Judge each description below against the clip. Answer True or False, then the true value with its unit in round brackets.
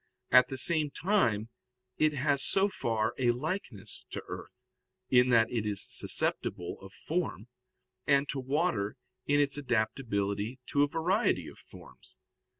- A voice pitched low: True (130 Hz)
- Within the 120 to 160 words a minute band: True (145 wpm)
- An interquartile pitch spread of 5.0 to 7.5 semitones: True (5.3 semitones)